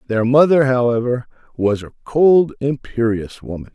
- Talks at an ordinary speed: No, slow, 130 wpm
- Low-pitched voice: Yes, low, 125 Hz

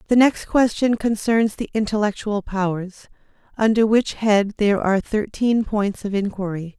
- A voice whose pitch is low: No, high, 210 Hz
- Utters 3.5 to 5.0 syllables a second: Yes, 4.7 syllables/s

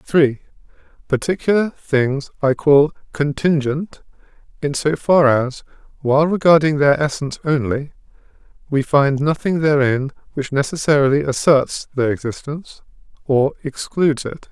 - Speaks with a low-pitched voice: No, medium, 145 Hz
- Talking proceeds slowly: Yes, slow, 110 wpm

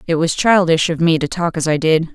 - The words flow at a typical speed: No, fast, 280 wpm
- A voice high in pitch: No, medium, 165 Hz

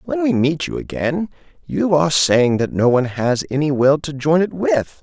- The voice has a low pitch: No, medium, 145 Hz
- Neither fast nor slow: No, fast, 215 wpm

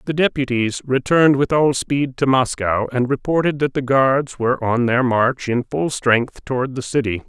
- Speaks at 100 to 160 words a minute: No, average, 190 wpm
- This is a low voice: Yes, low, 130 Hz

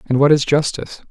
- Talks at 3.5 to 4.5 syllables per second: No, 6.5 syllables/s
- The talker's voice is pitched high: No, medium, 140 Hz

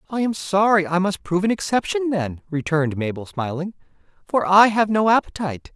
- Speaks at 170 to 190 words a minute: Yes, average, 175 wpm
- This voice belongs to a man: Yes, male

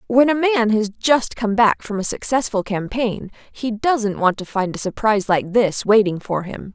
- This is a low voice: No, high, 215 Hz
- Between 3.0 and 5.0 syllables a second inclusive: Yes, 4.5 syllables/s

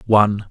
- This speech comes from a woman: No, male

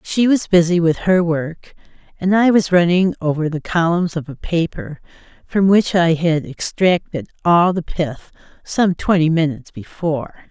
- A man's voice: No, female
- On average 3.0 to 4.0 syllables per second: No, 4.5 syllables/s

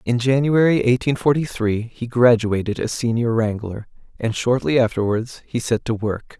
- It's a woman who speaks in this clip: No, male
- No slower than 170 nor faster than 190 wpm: No, average, 160 wpm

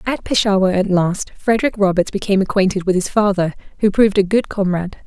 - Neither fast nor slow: Yes, average, 190 wpm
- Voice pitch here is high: Yes, high, 195 Hz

